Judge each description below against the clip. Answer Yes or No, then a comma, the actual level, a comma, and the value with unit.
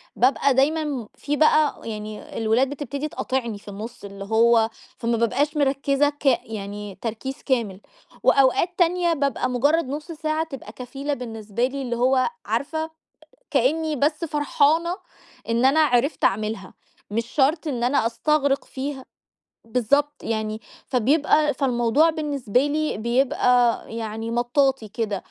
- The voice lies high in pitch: Yes, very high, 265 Hz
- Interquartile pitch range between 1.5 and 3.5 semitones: No, average, 4.2 semitones